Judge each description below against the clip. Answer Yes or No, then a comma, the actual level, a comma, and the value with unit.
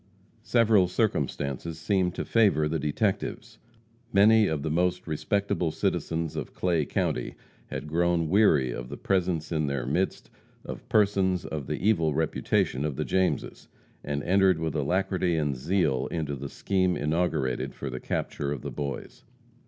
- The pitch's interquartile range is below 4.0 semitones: No, average, 4.4 semitones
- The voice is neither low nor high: No, very low, 80 Hz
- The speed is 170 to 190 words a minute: No, average, 155 wpm